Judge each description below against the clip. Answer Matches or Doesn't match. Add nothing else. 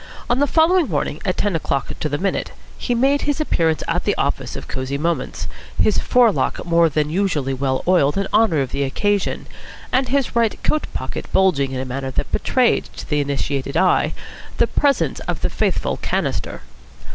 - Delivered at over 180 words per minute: Matches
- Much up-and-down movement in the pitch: Matches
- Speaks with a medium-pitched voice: Matches